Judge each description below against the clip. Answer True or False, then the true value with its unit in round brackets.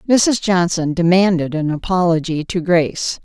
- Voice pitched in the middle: True (175 Hz)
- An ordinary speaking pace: False (130 wpm)